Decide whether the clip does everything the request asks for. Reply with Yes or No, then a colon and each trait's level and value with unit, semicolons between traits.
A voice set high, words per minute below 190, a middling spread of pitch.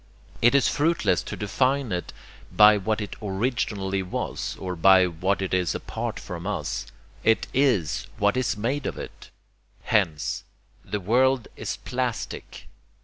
No: low, 105 Hz; average, 145 wpm; average, 5.0 semitones